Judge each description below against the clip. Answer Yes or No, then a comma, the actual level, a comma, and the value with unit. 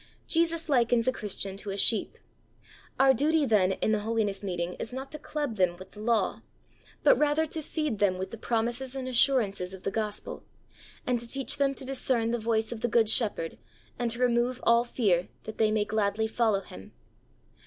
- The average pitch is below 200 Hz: No, high, 230 Hz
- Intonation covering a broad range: No, average, 4.0 semitones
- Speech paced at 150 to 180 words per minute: No, average, 195 wpm